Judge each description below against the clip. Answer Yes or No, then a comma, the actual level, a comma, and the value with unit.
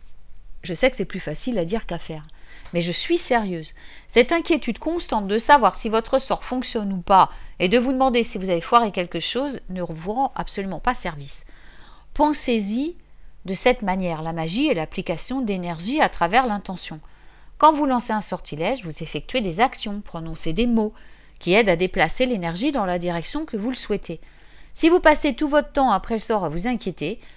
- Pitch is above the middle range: Yes, high, 210 Hz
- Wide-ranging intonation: Yes, wide, 6.7 semitones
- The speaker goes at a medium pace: Yes, average, 195 wpm